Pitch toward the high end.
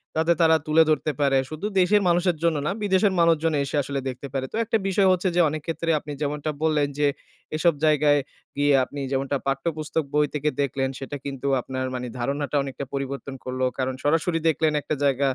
No: medium, 150 Hz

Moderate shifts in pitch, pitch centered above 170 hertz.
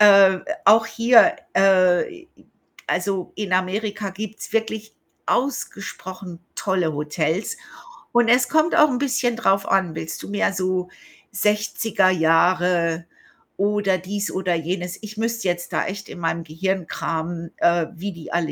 Yes: average, 3.4 semitones; high, 190 Hz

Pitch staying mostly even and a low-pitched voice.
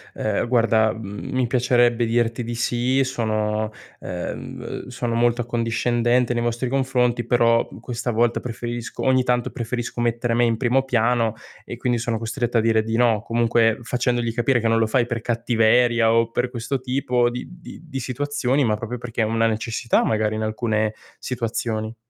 Yes: narrow, 1.4 semitones; low, 120 Hz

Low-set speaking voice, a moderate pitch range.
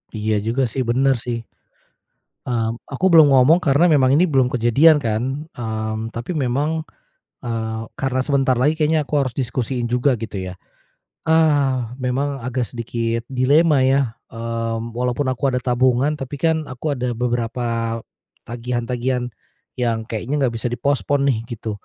Yes: low, 125 Hz; average, 3.2 semitones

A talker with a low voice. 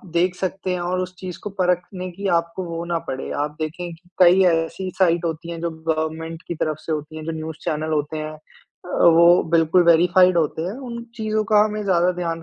No: medium, 170 Hz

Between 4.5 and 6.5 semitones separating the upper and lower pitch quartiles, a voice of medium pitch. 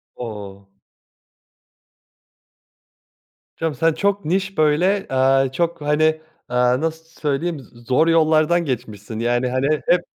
Yes: average, 4.8 semitones; medium, 150 Hz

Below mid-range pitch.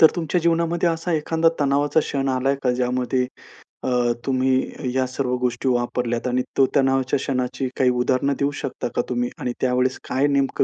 Yes: low, 130 Hz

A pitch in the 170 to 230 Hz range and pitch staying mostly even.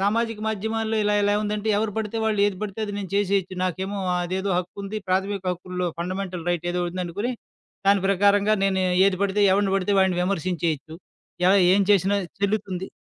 Yes: high, 195 Hz; narrow, 1.9 semitones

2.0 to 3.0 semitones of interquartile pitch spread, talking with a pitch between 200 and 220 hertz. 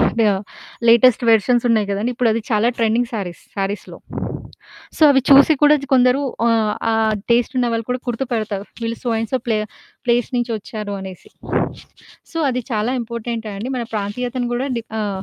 No: narrow, 2.6 semitones; high, 230 Hz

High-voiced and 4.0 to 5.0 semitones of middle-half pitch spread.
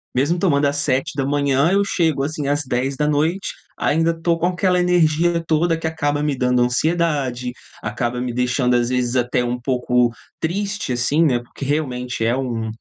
No: medium, 140 Hz; average, 4.7 semitones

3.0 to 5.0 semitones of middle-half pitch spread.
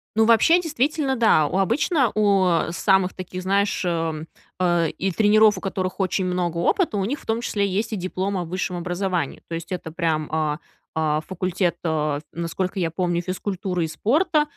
Yes: average, 3.4 semitones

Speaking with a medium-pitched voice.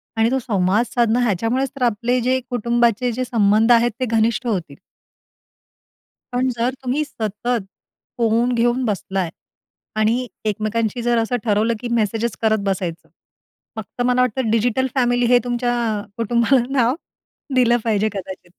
No: high, 235 Hz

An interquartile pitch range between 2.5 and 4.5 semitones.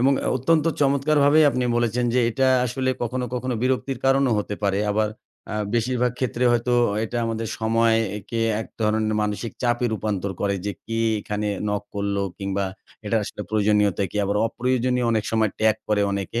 Yes: average, 3.2 semitones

